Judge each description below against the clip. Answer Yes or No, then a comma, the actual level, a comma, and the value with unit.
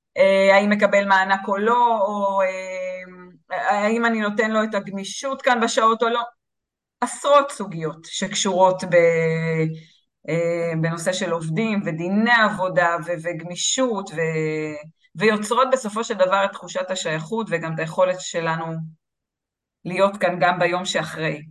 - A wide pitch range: No, average, 4.1 semitones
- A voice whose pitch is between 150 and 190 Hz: Yes, medium, 185 Hz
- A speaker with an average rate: Yes, average, 115 wpm